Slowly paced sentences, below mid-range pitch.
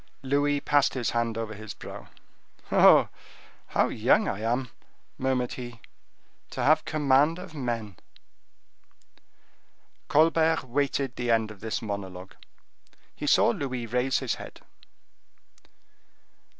Yes: slow, 115 wpm; low, 125 Hz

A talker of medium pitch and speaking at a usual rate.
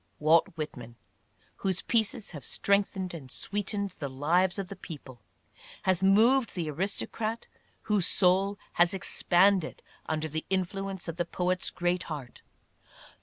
No: medium, 180 Hz; slow, 130 wpm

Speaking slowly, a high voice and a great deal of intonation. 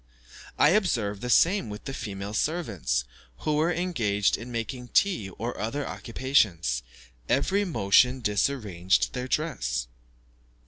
No: slow, 125 wpm; low, 120 Hz; wide, 6.8 semitones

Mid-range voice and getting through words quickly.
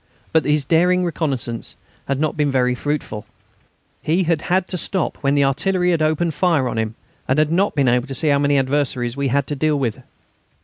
Yes: medium, 145 Hz; fast, 210 wpm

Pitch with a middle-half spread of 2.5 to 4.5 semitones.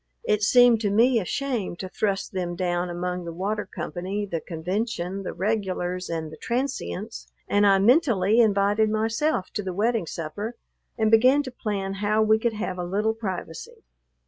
Yes: average, 3.6 semitones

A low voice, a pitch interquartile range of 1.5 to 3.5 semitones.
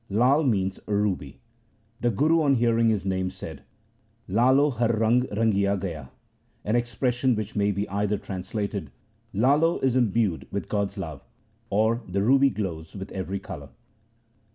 No: low, 105 Hz; average, 3.9 semitones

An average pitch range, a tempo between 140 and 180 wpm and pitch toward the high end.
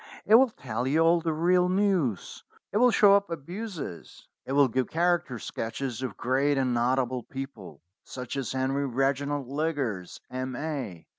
No: average, 4.7 semitones; average, 155 wpm; low, 135 Hz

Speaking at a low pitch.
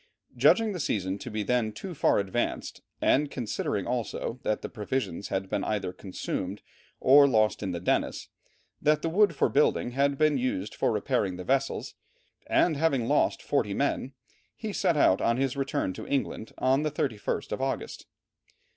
Yes: low, 125 Hz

